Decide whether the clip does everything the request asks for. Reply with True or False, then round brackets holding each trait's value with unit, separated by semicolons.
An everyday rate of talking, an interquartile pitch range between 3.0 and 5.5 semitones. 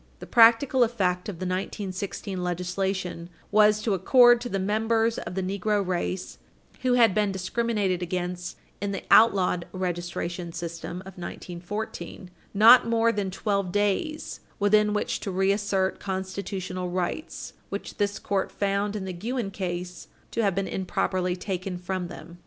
False (145 wpm; 2.6 semitones)